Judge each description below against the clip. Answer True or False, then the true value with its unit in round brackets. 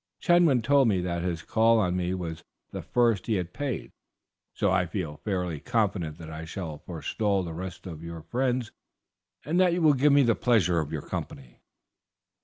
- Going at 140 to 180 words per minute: False (190 wpm)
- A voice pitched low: True (95 Hz)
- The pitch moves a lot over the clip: True (6.2 semitones)